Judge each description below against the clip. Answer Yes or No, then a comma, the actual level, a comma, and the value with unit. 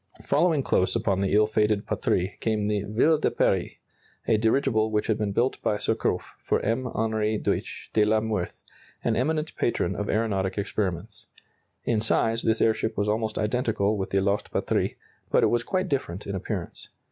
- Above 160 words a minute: Yes, average, 180 wpm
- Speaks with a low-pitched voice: Yes, low, 110 Hz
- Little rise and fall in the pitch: Yes, narrow, 2.0 semitones